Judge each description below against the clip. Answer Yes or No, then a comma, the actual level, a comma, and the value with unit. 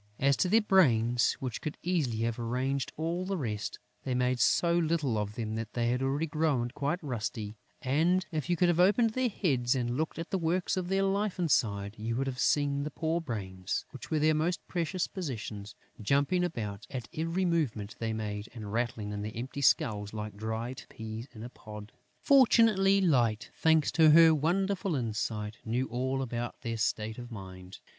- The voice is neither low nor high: No, low, 130 Hz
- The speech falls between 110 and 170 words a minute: No, average, 190 wpm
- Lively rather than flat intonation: Yes, wide, 7.0 semitones